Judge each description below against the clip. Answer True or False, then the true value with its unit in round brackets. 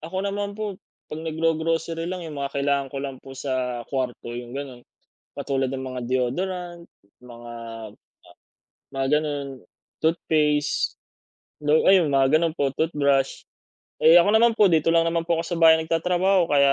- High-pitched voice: False (155 Hz)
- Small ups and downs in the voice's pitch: False (3.8 semitones)